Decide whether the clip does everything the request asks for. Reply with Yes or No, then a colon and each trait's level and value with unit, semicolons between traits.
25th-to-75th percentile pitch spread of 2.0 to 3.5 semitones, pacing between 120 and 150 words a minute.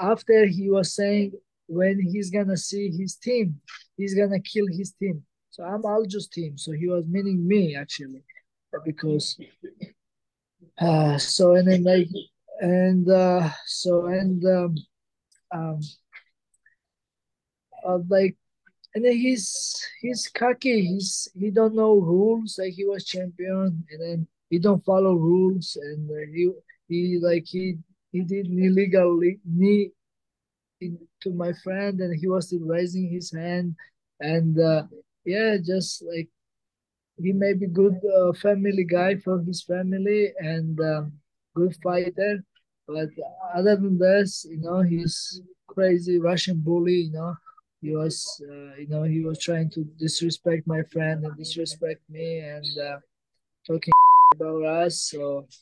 Yes: average, 3.1 semitones; average, 140 wpm